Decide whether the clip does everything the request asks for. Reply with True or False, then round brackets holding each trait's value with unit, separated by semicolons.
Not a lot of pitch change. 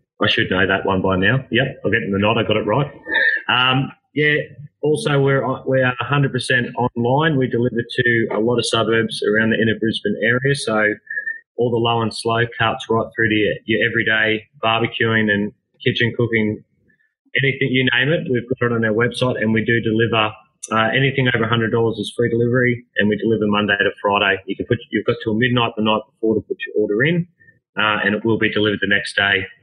False (3.0 semitones)